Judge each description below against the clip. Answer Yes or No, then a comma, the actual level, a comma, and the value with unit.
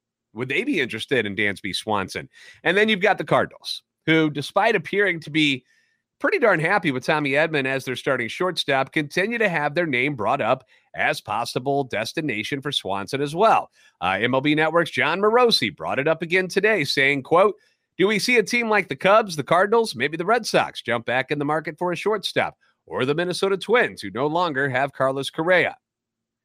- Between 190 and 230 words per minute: Yes, average, 195 wpm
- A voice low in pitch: No, medium, 155 Hz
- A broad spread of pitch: Yes, wide, 6.3 semitones